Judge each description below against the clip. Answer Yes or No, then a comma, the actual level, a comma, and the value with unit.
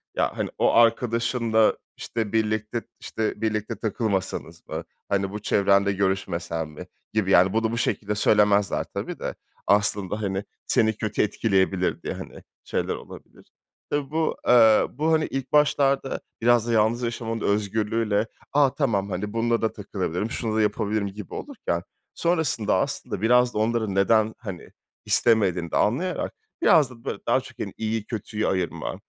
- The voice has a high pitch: No, low, 110 Hz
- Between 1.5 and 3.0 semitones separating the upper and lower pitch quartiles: Yes, average, 2.7 semitones